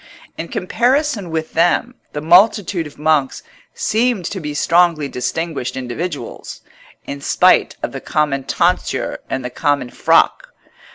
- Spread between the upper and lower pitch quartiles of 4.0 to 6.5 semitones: Yes, average, 4.5 semitones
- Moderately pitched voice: Yes, medium, 160 Hz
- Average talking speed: No, slow, 130 wpm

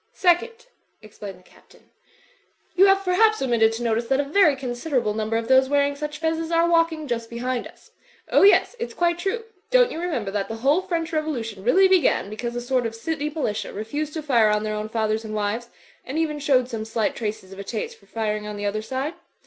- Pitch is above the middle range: Yes, very high, 255 Hz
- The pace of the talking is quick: Yes, fast, 230 wpm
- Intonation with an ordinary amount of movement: No, wide, 6.7 semitones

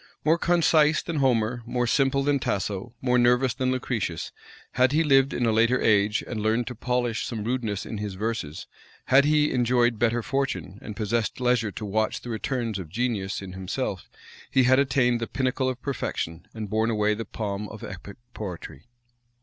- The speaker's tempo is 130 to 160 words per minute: No, average, 180 wpm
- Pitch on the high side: No, low, 120 Hz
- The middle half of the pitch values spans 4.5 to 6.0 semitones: No, average, 3.5 semitones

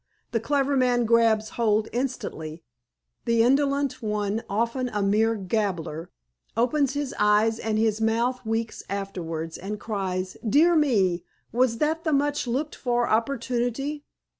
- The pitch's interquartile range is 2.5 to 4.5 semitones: Yes, average, 3.8 semitones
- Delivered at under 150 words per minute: Yes, slow, 135 wpm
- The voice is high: Yes, high, 230 Hz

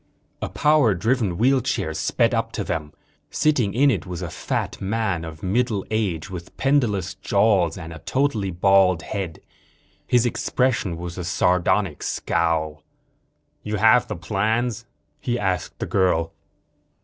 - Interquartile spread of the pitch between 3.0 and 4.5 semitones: No, average, 5.3 semitones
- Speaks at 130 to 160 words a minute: Yes, average, 140 wpm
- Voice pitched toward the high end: No, low, 100 Hz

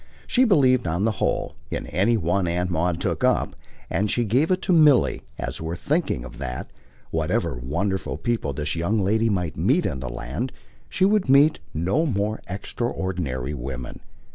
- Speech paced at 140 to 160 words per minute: No, average, 170 wpm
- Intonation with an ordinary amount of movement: No, wide, 7.6 semitones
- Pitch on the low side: Yes, very low, 95 Hz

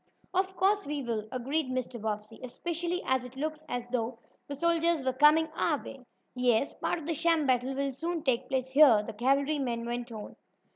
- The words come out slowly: No, average, 190 wpm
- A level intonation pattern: No, average, 4.4 semitones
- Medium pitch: No, very high, 270 Hz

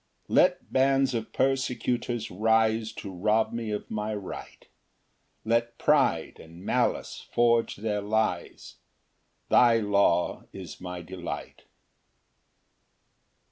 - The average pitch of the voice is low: Yes, low, 110 Hz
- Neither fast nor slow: No, slow, 105 wpm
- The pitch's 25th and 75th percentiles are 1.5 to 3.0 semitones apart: Yes, average, 2.7 semitones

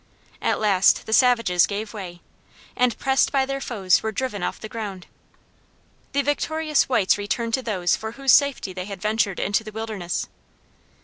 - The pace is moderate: Yes, average, 170 wpm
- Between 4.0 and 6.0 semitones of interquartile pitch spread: Yes, average, 4.8 semitones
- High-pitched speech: Yes, high, 220 Hz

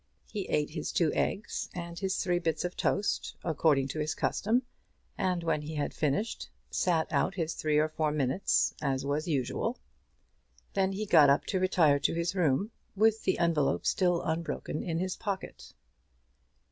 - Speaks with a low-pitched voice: No, medium, 170 Hz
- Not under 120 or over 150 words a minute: No, average, 170 wpm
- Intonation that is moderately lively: Yes, average, 3.8 semitones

